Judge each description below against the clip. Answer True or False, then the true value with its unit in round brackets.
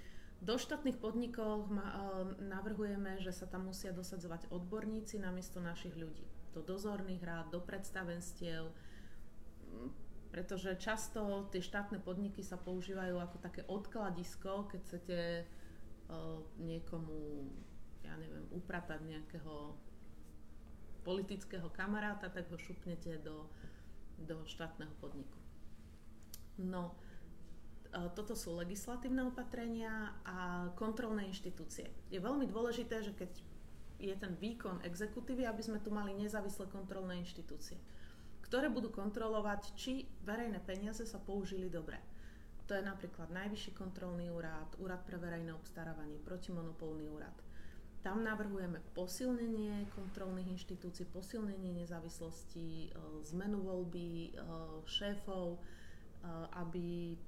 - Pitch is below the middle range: False (180 Hz)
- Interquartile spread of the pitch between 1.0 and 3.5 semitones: False (3.9 semitones)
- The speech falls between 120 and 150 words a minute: False (110 wpm)